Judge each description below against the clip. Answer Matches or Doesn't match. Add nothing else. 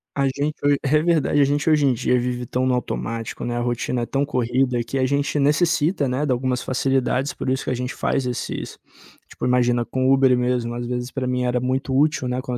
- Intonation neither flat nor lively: Doesn't match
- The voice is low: Matches